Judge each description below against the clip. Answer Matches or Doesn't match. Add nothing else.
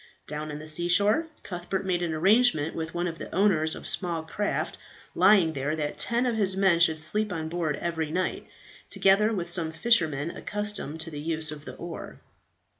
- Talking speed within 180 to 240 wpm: Matches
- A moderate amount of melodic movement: Matches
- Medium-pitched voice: Matches